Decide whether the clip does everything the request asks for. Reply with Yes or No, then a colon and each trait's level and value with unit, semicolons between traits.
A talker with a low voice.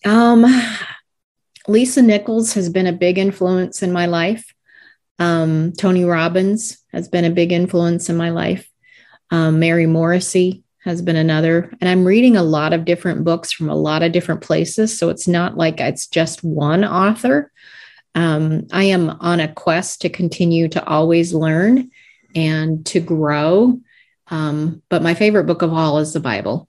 No: medium, 175 Hz